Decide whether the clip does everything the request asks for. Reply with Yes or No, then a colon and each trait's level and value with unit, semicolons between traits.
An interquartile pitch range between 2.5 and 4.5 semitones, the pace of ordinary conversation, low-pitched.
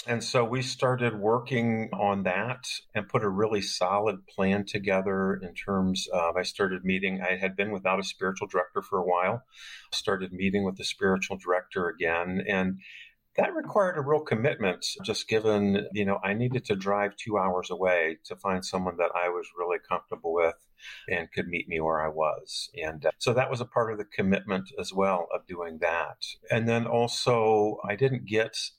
Yes: average, 3.3 semitones; average, 190 wpm; low, 100 Hz